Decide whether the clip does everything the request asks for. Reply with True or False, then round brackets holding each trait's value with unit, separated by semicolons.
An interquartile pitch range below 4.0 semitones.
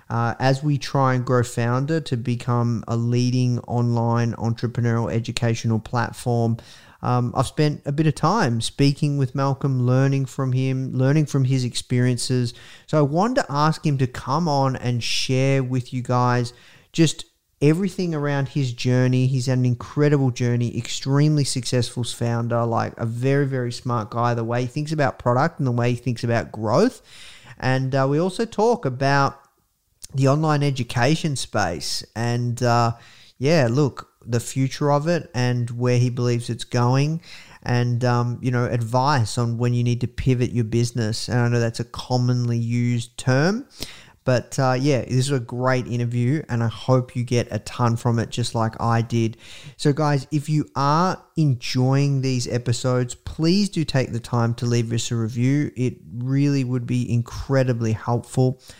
True (2.5 semitones)